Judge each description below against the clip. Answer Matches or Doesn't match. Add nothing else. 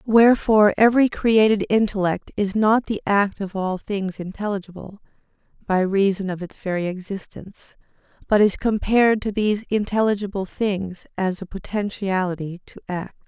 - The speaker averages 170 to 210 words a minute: Doesn't match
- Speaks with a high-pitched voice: Matches